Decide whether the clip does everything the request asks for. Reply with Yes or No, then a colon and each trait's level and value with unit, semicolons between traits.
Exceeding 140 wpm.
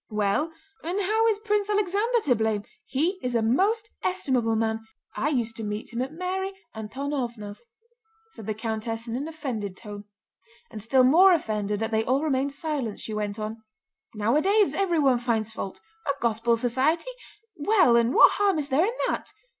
Yes: average, 170 wpm